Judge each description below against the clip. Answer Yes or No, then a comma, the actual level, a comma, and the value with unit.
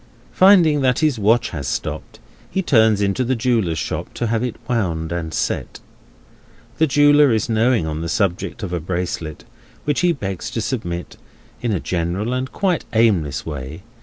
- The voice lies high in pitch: No, low, 110 Hz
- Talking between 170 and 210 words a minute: Yes, average, 175 wpm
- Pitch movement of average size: No, wide, 6.9 semitones